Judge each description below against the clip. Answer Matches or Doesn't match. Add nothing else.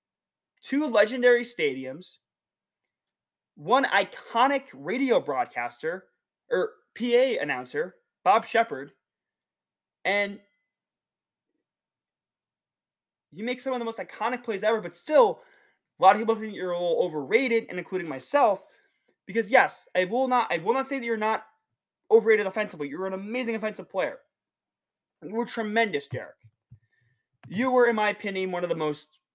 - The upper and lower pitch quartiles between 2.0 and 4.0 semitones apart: Doesn't match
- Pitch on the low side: Doesn't match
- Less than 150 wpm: Matches